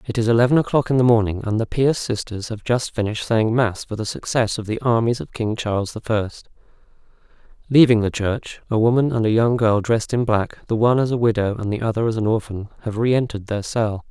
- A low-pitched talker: Yes, low, 115 Hz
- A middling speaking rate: No, fast, 230 wpm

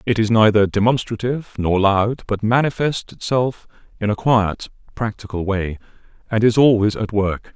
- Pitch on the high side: No, low, 110 Hz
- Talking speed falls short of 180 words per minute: Yes, average, 150 wpm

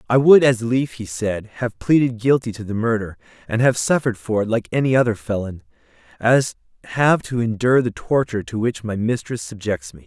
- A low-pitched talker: Yes, low, 115 Hz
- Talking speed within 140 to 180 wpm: No, average, 195 wpm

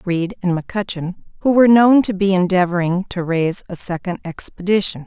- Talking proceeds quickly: No, average, 165 wpm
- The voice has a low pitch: No, high, 190 Hz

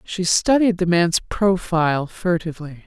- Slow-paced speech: Yes, slow, 125 wpm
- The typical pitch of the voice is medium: Yes, medium, 175 Hz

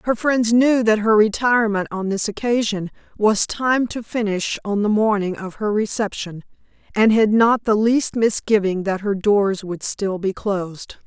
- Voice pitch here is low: No, high, 210 Hz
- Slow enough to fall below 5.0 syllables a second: Yes, 4.5 syllables/s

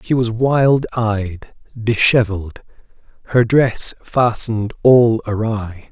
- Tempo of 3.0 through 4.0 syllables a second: Yes, 3.4 syllables/s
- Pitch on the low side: Yes, low, 115 Hz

